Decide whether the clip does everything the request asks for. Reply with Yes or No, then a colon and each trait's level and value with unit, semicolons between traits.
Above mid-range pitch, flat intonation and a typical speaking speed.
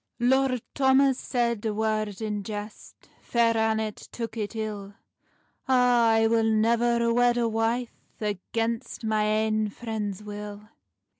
No: high, 225 Hz; narrow, 1.8 semitones; slow, 130 wpm